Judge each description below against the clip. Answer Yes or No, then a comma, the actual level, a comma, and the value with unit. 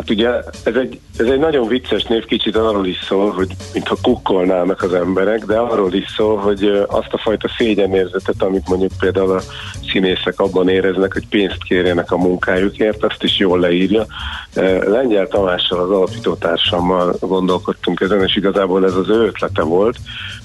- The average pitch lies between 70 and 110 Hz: Yes, very low, 95 Hz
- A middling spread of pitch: No, narrow, 1.9 semitones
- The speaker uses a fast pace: Yes, fast, 165 wpm